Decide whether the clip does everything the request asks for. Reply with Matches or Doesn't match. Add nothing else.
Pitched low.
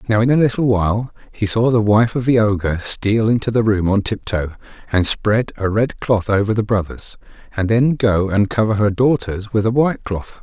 Matches